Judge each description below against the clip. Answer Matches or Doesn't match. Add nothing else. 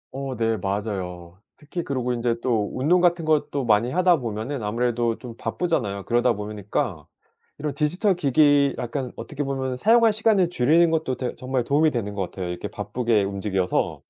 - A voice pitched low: Matches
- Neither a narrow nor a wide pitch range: Doesn't match